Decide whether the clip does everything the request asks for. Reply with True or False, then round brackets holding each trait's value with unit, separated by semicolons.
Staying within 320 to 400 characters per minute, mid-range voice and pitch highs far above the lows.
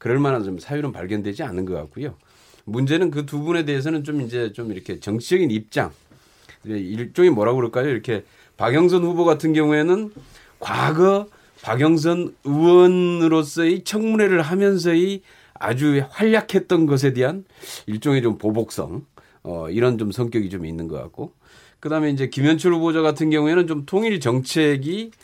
True (330 characters per minute; 150 Hz; 6.7 semitones)